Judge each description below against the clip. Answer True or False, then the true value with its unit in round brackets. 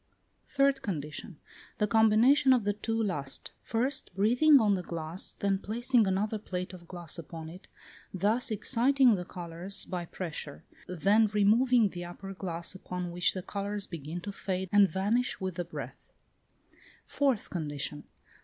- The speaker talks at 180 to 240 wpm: False (150 wpm)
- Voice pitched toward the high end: True (195 Hz)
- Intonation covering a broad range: False (4.1 semitones)